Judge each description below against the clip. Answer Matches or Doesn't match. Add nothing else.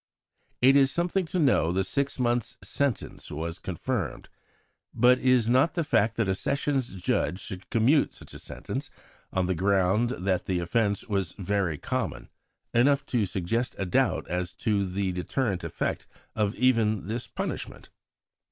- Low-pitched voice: Matches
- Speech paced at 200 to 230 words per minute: Doesn't match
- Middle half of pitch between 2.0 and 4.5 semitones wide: Doesn't match